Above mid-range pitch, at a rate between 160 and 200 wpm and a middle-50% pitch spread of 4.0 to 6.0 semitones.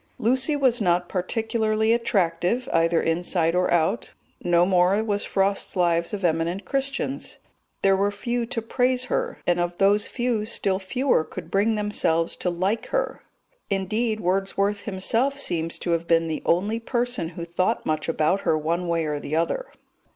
Yes: high, 195 Hz; average, 165 wpm; average, 4.9 semitones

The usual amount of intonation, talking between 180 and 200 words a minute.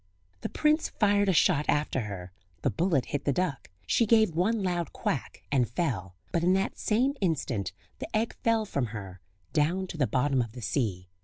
No: wide, 8.3 semitones; average, 190 wpm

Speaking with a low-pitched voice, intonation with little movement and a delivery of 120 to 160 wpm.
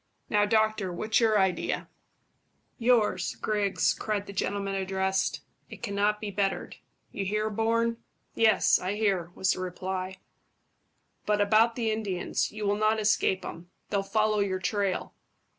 No: high, 205 Hz; narrow, 2.2 semitones; average, 140 wpm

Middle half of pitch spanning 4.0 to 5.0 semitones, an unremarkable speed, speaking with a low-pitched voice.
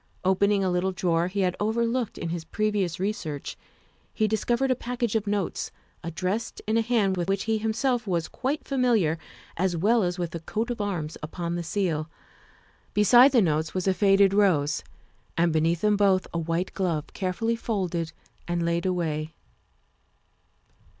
No: average, 4.3 semitones; average, 170 wpm; high, 190 Hz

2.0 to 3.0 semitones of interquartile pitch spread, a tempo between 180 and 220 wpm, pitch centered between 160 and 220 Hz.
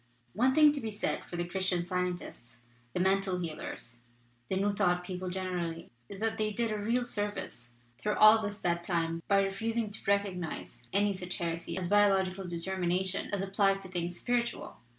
Yes: average, 2.7 semitones; average, 185 wpm; high, 190 Hz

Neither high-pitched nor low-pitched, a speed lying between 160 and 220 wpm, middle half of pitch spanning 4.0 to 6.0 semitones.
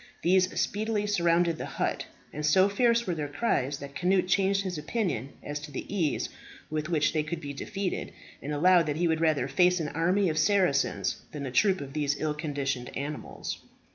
Yes: medium, 165 Hz; average, 195 wpm; average, 4.3 semitones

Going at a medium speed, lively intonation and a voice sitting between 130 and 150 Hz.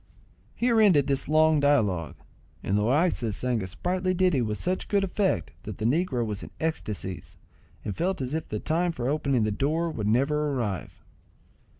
Yes: average, 175 wpm; wide, 7.7 semitones; medium, 140 Hz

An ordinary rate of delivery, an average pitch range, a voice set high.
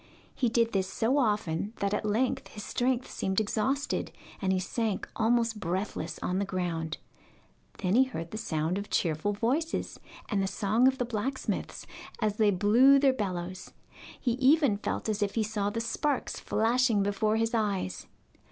Yes: average, 170 wpm; average, 3.7 semitones; high, 215 Hz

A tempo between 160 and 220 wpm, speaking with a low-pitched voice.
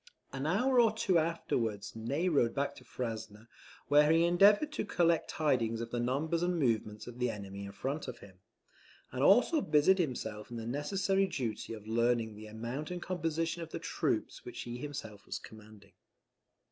Yes: average, 180 wpm; low, 130 Hz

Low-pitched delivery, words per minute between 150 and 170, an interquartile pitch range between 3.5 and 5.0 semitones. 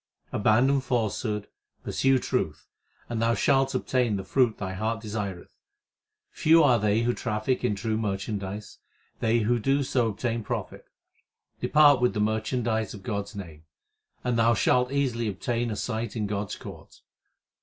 No: low, 115 Hz; average, 155 wpm; average, 3.0 semitones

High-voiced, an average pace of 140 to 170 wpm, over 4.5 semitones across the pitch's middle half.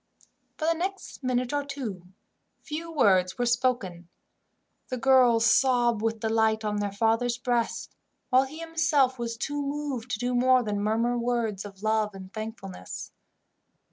No: high, 240 Hz; average, 150 wpm; average, 3.3 semitones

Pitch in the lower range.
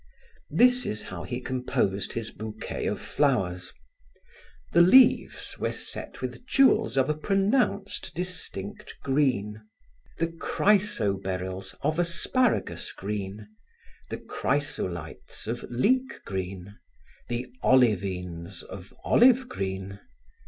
Yes: low, 120 Hz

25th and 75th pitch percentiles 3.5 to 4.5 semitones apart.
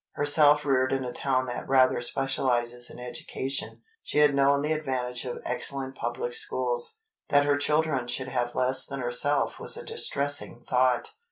No: narrow, 2.4 semitones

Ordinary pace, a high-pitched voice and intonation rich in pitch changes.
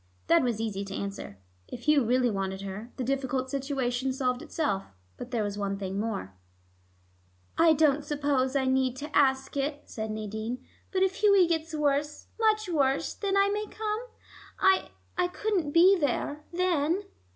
Yes: average, 160 wpm; very high, 275 Hz; wide, 6.6 semitones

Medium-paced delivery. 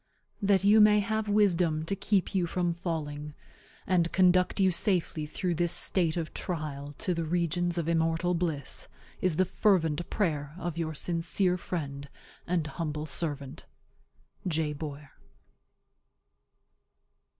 No: slow, 130 wpm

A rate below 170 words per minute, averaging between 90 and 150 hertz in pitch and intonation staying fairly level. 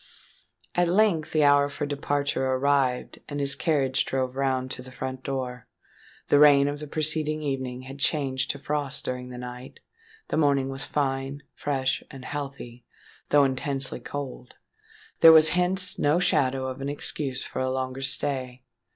Yes: average, 160 wpm; medium, 140 Hz; narrow, 2.0 semitones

